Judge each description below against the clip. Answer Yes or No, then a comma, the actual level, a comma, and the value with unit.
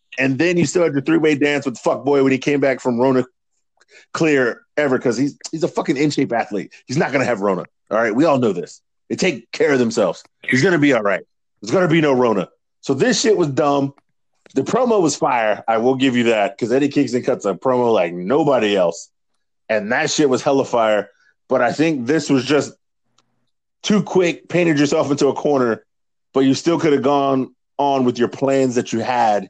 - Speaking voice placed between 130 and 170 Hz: Yes, low, 135 Hz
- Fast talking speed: Yes, fast, 230 wpm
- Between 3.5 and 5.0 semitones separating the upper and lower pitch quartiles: No, average, 3.1 semitones